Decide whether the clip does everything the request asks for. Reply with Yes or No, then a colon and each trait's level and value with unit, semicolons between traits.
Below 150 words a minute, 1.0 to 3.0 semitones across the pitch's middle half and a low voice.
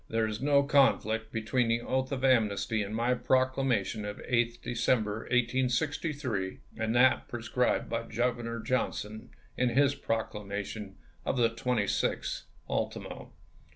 Yes: slow, 135 wpm; average, 2.7 semitones; low, 120 Hz